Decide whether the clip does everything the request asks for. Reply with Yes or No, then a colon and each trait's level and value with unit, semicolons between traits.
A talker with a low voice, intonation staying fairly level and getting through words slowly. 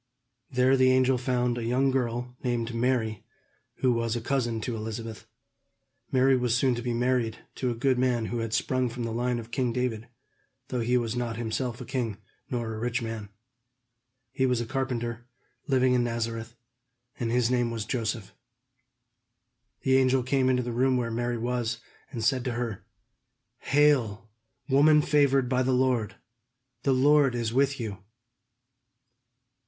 No: low, 125 Hz; narrow, 1.9 semitones; average, 165 wpm